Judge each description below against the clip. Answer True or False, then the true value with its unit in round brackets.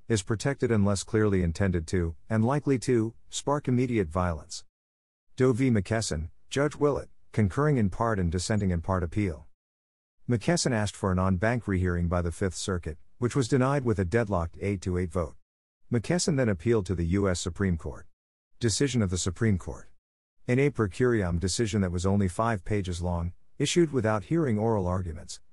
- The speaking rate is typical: True (170 wpm)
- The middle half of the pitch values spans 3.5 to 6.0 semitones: True (5.0 semitones)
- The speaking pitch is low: True (100 Hz)